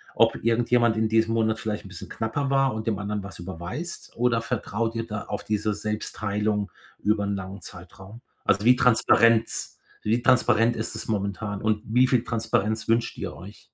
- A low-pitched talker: Yes, low, 110 Hz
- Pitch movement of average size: No, narrow, 2.1 semitones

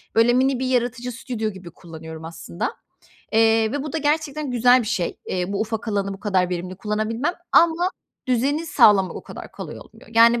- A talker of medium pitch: No, high, 225 Hz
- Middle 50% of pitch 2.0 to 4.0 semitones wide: No, average, 4.7 semitones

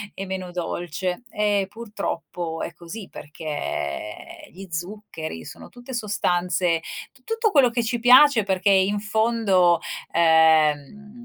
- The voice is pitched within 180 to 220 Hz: Yes, high, 190 Hz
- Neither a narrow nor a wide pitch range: Yes, average, 4.8 semitones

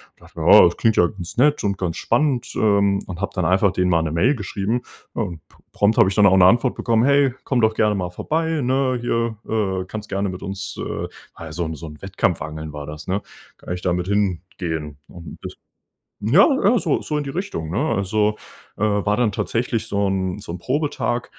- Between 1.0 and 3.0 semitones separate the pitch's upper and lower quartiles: No, average, 4.9 semitones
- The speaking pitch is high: No, low, 100 Hz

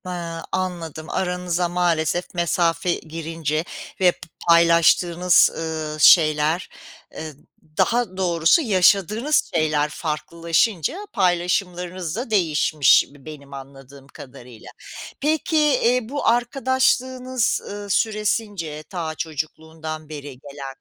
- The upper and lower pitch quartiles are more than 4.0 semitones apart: No, average, 3.5 semitones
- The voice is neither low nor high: Yes, medium, 170 Hz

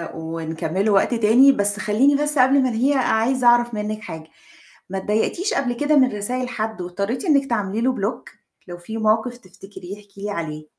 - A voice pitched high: Yes, high, 220 Hz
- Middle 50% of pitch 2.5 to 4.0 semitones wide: No, average, 4.5 semitones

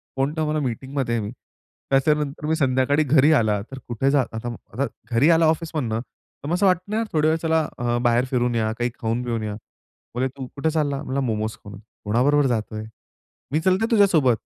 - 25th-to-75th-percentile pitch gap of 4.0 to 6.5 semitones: Yes, average, 4.7 semitones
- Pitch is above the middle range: No, low, 135 Hz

